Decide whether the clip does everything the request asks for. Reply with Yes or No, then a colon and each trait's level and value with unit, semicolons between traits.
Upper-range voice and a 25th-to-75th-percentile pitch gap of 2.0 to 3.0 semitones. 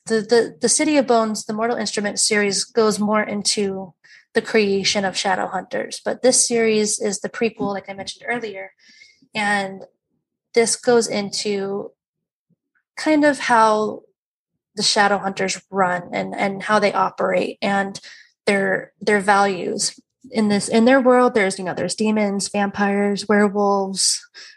Yes: high, 210 Hz; average, 2.7 semitones